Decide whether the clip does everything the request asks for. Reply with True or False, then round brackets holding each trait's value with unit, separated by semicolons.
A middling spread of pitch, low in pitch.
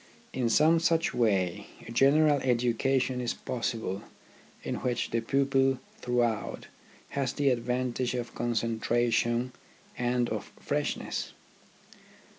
False (2.3 semitones; 125 Hz)